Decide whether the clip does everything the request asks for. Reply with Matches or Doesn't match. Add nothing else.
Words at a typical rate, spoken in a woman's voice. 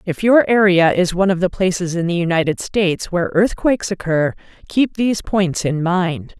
Matches